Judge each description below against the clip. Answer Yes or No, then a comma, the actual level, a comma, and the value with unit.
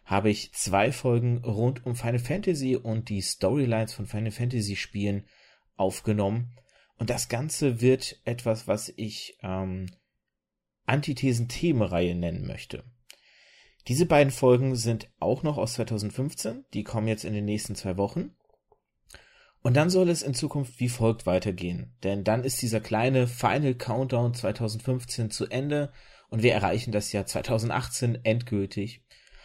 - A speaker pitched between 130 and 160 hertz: No, low, 115 Hz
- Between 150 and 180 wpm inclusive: No, average, 140 wpm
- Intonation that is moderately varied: Yes, average, 3.5 semitones